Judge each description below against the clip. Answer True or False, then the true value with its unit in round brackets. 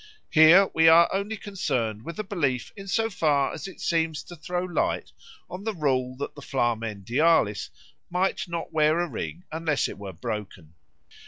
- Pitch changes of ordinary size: False (5.9 semitones)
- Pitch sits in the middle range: True (160 Hz)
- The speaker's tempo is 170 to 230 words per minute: True (175 wpm)